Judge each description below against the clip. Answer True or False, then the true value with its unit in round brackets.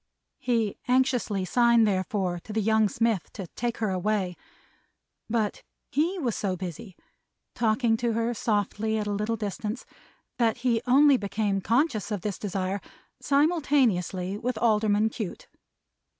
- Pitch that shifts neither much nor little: True (3.0 semitones)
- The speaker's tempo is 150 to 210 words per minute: False (135 wpm)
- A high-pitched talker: True (220 Hz)